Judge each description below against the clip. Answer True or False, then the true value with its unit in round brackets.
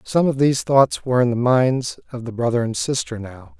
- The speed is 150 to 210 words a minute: False (235 wpm)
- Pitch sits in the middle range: False (125 Hz)